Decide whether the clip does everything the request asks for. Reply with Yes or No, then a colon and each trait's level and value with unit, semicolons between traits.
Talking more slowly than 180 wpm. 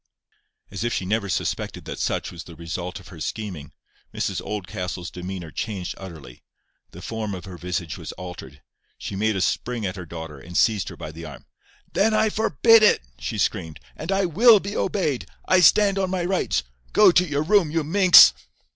No: average, 195 wpm